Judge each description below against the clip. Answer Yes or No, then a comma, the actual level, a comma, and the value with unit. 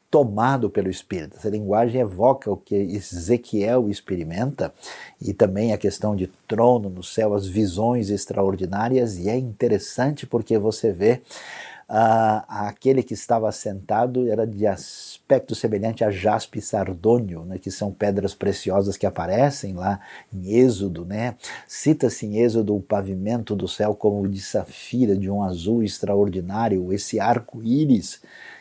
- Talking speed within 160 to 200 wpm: No, average, 140 wpm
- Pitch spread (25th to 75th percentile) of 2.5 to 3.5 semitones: Yes, average, 2.9 semitones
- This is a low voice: Yes, low, 105 Hz